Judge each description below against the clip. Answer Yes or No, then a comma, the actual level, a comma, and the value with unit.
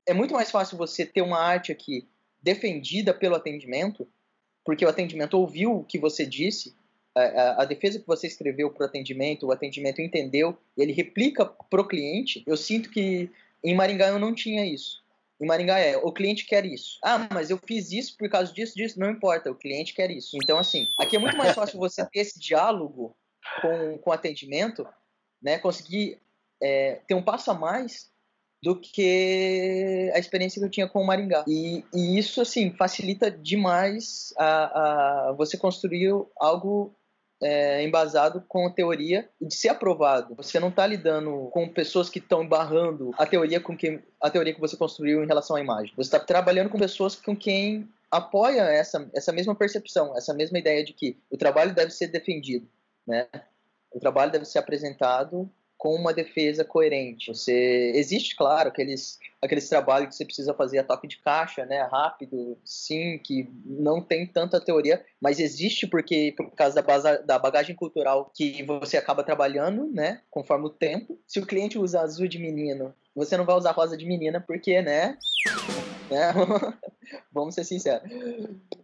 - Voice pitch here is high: No, medium, 170 Hz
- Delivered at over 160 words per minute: Yes, average, 180 wpm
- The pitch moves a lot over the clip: No, average, 4.7 semitones